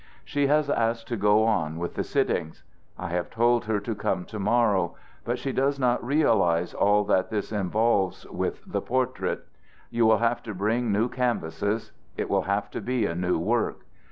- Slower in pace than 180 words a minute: No, average, 185 wpm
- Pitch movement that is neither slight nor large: Yes, average, 3.7 semitones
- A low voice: Yes, low, 110 Hz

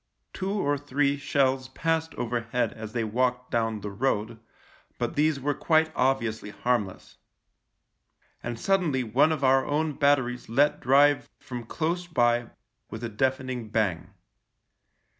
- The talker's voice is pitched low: Yes, low, 130 Hz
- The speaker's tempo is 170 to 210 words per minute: No, slow, 135 wpm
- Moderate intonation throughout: Yes, average, 3.8 semitones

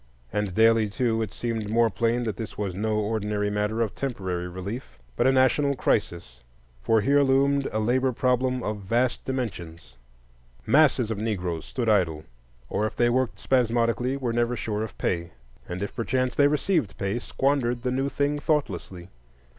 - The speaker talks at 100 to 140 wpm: No, average, 170 wpm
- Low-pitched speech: Yes, low, 115 Hz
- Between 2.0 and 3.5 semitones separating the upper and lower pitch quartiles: No, average, 3.9 semitones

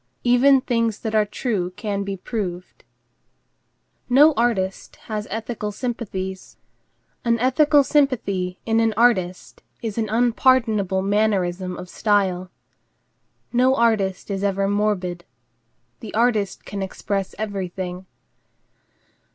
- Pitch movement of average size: Yes, average, 3.7 semitones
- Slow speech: Yes, slow, 110 wpm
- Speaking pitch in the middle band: No, high, 210 Hz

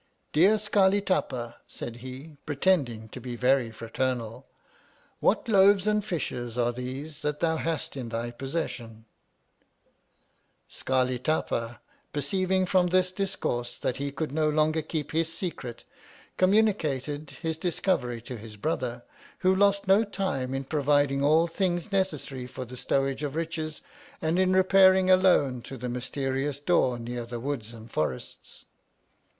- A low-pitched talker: No, medium, 145 Hz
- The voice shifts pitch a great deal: Yes, wide, 6.5 semitones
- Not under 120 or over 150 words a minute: Yes, average, 145 wpm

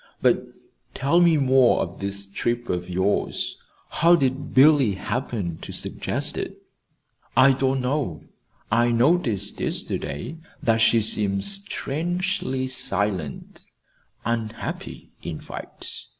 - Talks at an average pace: No, slow, 110 wpm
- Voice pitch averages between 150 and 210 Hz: No, low, 120 Hz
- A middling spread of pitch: No, wide, 5.7 semitones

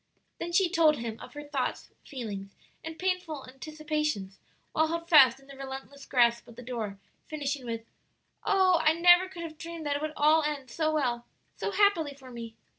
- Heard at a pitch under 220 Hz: No, very high, 295 Hz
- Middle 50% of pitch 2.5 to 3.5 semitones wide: No, average, 4.4 semitones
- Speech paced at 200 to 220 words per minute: No, average, 190 wpm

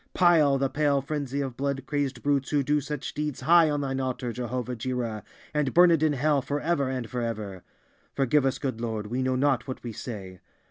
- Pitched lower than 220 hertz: Yes, low, 135 Hz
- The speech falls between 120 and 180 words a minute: No, average, 195 wpm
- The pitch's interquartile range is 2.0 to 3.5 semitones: Yes, average, 2.9 semitones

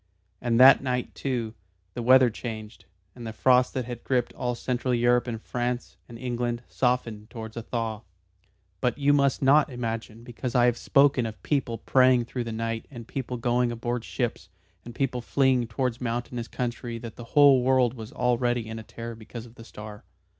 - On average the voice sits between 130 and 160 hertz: No, low, 120 Hz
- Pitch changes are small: Yes, narrow, 1.6 semitones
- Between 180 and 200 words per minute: Yes, average, 185 wpm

